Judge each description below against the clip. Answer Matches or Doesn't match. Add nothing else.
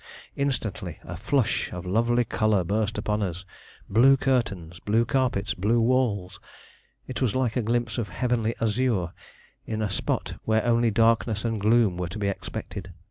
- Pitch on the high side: Doesn't match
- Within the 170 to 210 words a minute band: Doesn't match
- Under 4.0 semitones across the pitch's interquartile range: Matches